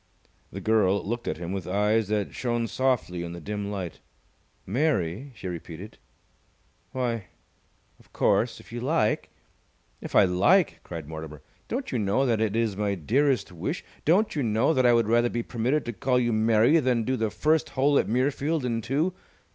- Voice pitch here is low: Yes, low, 115 Hz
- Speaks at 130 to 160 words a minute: No, average, 185 wpm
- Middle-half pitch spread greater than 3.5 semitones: Yes, average, 4.7 semitones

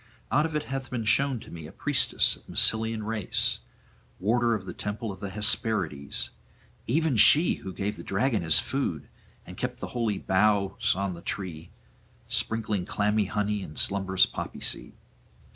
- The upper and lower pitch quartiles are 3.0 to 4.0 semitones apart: Yes, average, 3.6 semitones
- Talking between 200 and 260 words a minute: No, average, 165 wpm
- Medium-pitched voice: No, low, 105 Hz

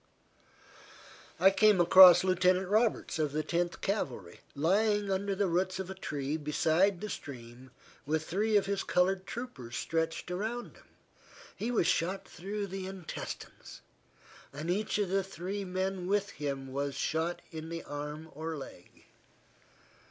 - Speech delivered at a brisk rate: No, average, 145 wpm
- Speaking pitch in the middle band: Yes, medium, 180 Hz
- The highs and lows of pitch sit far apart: No, average, 4.0 semitones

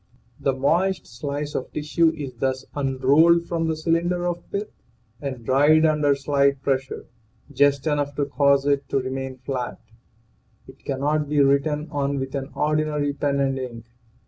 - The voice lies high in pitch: No, medium, 140 Hz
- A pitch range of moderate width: No, narrow, 2.1 semitones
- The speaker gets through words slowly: No, average, 155 wpm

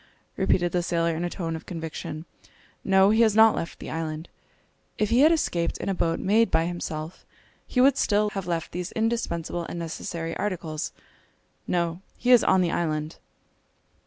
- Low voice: No, medium, 175 Hz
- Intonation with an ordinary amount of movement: Yes, average, 4.0 semitones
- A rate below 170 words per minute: No, average, 180 wpm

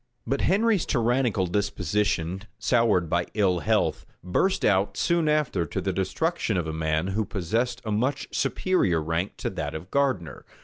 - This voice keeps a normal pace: Yes, average, 160 wpm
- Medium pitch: No, low, 100 Hz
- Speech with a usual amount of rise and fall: No, wide, 7.1 semitones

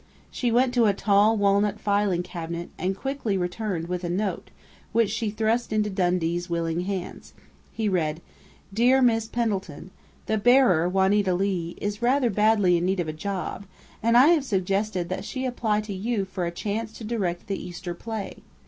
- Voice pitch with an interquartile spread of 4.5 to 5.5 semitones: No, average, 3.7 semitones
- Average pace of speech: Yes, average, 175 wpm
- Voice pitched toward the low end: No, high, 200 Hz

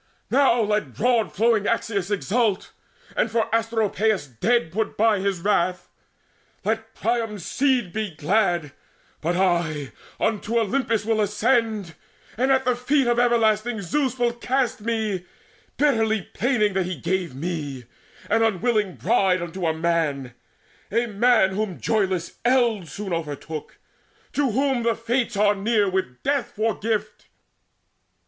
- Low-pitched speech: No, high, 215 Hz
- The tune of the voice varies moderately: Yes, average, 4.1 semitones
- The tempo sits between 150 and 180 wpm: No, slow, 135 wpm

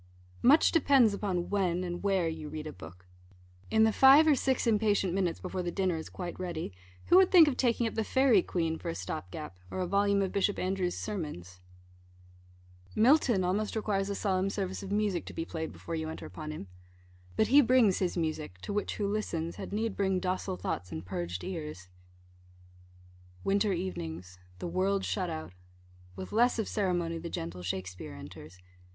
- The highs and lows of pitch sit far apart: No, average, 4.7 semitones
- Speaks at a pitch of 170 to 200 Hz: Yes, medium, 185 Hz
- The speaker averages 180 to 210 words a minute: Yes, average, 185 wpm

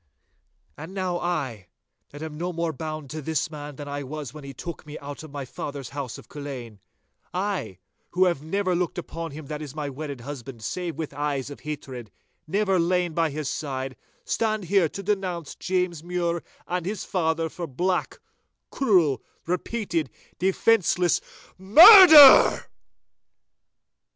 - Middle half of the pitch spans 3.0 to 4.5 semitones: Yes, average, 4.1 semitones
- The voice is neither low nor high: Yes, medium, 160 Hz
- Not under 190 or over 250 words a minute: No, average, 150 wpm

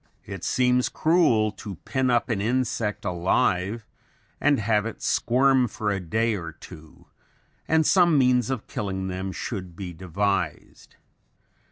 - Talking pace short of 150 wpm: Yes, average, 140 wpm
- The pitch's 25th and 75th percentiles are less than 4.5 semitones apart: No, average, 5.0 semitones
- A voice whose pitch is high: No, low, 110 Hz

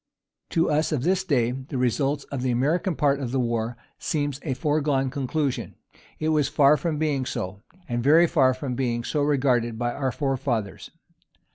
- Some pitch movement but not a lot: Yes, average, 3.3 semitones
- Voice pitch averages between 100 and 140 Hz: Yes, low, 135 Hz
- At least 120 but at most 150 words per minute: No, average, 175 wpm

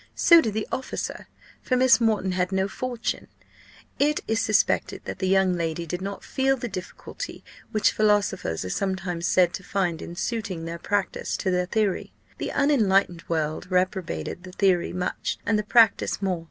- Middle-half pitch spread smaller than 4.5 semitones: Yes, average, 3.4 semitones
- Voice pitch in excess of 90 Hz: Yes, high, 190 Hz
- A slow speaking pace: No, average, 170 wpm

